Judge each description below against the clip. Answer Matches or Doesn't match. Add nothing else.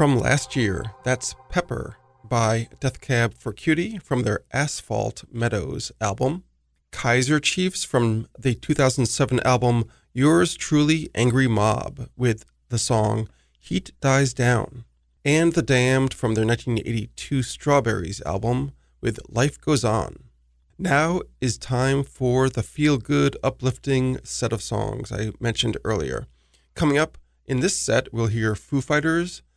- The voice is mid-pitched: Doesn't match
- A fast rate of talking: Doesn't match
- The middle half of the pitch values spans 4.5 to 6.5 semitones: Doesn't match